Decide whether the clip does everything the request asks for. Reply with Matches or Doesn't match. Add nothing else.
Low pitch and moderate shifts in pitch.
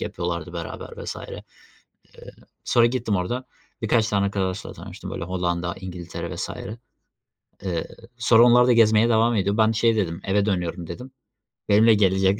Matches